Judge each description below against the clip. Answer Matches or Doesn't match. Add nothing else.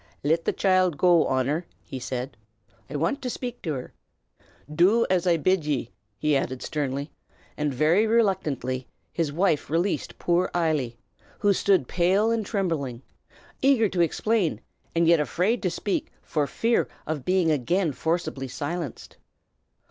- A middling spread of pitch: Matches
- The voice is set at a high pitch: Doesn't match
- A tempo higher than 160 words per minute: Doesn't match